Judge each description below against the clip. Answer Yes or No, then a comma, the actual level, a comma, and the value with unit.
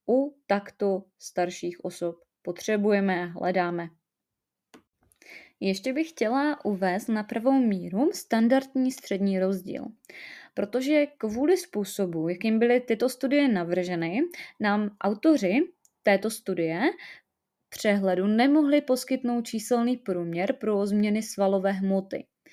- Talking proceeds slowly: Yes, slow, 100 wpm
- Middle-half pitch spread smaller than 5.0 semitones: No, wide, 5.6 semitones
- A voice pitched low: No, high, 215 Hz